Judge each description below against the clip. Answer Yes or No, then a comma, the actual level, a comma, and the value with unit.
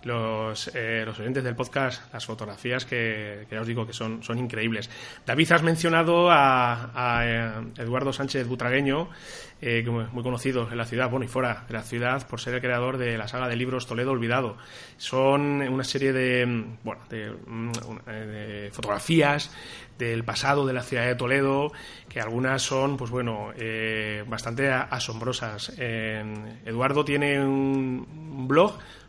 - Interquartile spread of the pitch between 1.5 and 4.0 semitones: Yes, average, 2.7 semitones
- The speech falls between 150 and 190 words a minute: Yes, average, 155 wpm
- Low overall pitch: Yes, low, 125 Hz